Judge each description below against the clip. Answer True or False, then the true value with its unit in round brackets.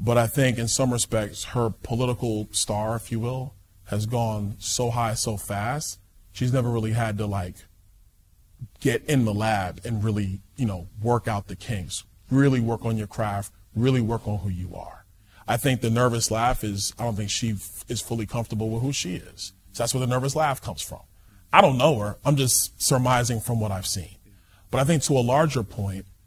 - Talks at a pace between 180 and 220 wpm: True (205 wpm)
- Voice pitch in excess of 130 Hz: False (110 Hz)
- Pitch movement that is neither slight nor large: True (3.6 semitones)